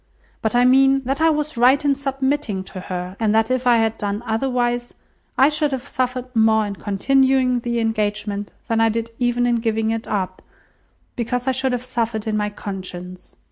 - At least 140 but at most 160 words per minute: No, average, 190 wpm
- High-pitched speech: Yes, high, 235 Hz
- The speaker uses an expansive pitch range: No, average, 3.4 semitones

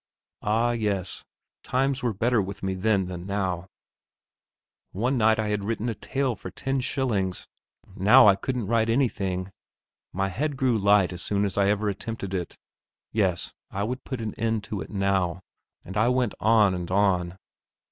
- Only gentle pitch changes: No, average, 3.5 semitones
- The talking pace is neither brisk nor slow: Yes, average, 170 wpm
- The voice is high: No, low, 105 Hz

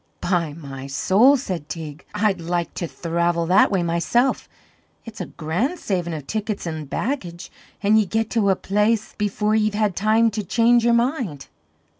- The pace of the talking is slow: No, average, 170 wpm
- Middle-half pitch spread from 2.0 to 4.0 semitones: No, average, 4.7 semitones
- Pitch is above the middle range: Yes, high, 195 Hz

